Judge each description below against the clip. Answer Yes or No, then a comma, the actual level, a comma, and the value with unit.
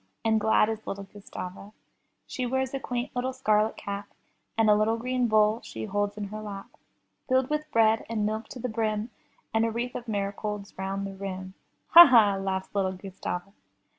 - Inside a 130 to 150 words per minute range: No, average, 185 wpm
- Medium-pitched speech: No, high, 215 Hz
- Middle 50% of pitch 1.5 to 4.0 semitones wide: Yes, average, 2.9 semitones